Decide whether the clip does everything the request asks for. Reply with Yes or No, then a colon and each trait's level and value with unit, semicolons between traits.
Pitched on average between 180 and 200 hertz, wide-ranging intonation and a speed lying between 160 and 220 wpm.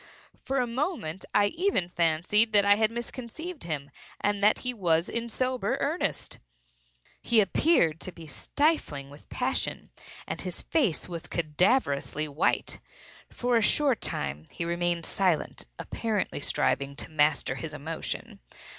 No: high, 190 Hz; wide, 7.2 semitones; average, 140 wpm